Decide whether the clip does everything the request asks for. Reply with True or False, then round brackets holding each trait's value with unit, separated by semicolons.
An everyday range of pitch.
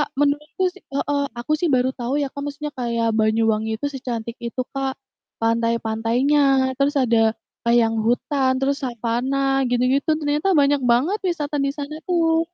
True (3.6 semitones)